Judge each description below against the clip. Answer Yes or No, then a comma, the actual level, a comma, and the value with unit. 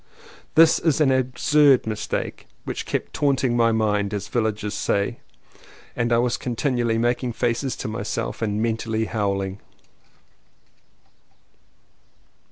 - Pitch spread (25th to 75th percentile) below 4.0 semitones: Yes, average, 2.8 semitones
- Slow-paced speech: Yes, slow, 105 wpm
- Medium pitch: No, low, 115 Hz